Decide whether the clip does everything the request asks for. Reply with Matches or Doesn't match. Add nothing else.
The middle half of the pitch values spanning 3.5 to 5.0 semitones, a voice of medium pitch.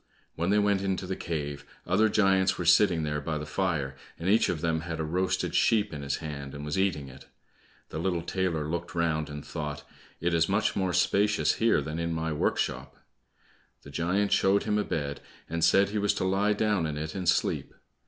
Doesn't match